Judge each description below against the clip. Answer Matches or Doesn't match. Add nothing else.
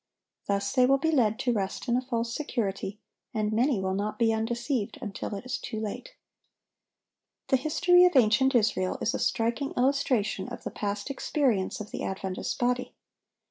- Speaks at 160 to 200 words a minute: Matches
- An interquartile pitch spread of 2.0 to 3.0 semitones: Doesn't match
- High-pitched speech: Matches